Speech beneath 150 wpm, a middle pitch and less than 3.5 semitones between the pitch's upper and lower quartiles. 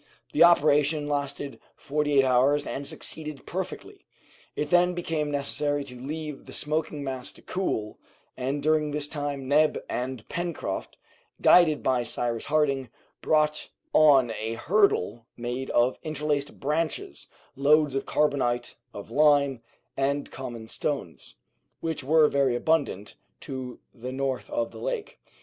Yes: slow, 135 wpm; medium, 145 Hz; average, 2.8 semitones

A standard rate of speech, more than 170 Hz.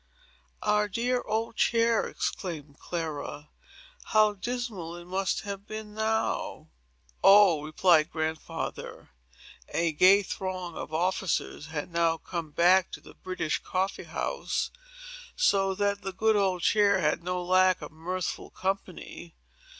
No: slow, 125 wpm; medium, 185 Hz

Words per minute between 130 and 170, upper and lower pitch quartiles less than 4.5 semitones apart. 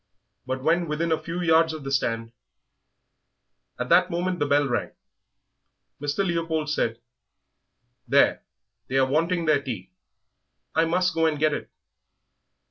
Yes: average, 145 wpm; average, 3.4 semitones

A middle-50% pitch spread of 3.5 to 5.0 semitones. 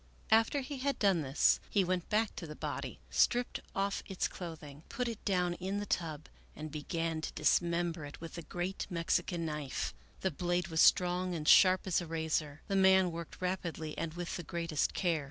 No: average, 2.8 semitones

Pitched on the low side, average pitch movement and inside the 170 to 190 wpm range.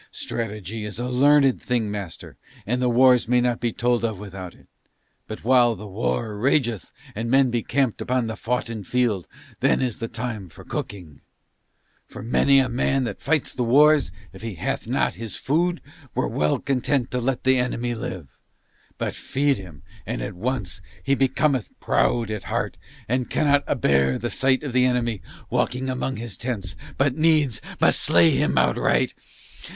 Yes: low, 120 Hz; average, 3.8 semitones; average, 175 wpm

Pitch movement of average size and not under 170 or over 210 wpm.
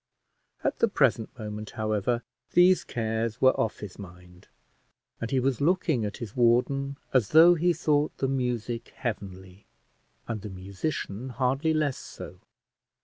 No: average, 4.5 semitones; average, 145 wpm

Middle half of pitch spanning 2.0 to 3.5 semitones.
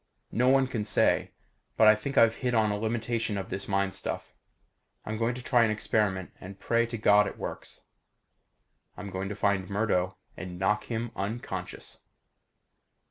Yes: average, 3.0 semitones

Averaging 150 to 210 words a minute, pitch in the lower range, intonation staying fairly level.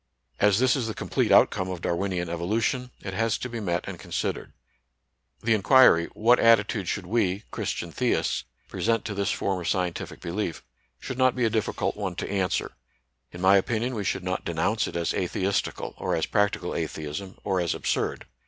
No: average, 185 wpm; low, 100 Hz; average, 4.0 semitones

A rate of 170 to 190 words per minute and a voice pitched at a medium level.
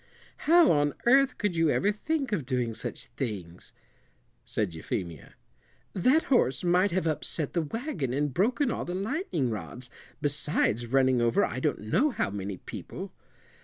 No: average, 155 wpm; medium, 150 Hz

